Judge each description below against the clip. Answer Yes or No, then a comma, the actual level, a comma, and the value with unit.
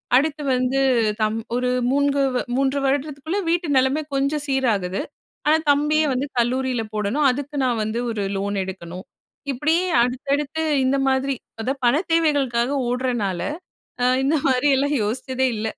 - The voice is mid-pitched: No, very high, 265 Hz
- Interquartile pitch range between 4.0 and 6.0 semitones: No, average, 3.2 semitones